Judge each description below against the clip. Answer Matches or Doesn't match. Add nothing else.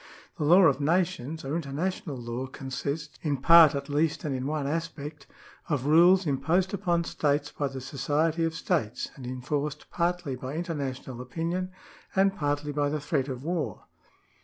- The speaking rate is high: Doesn't match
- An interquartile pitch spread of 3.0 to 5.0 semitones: Matches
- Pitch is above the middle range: Doesn't match